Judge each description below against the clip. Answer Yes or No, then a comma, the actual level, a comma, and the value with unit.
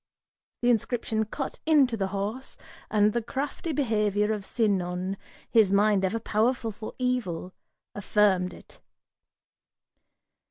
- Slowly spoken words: Yes, slow, 115 wpm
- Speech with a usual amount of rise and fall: Yes, average, 3.3 semitones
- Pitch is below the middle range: No, high, 215 Hz